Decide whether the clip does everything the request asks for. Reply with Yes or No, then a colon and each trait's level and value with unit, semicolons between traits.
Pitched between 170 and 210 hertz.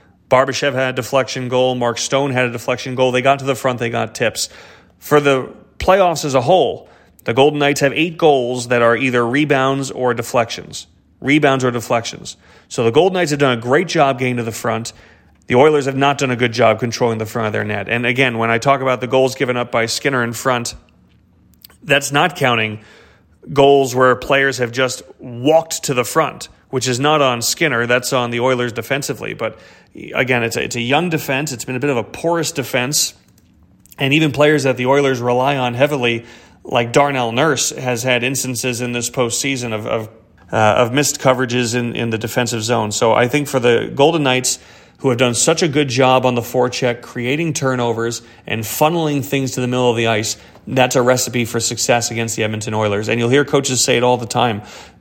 No: low, 125 Hz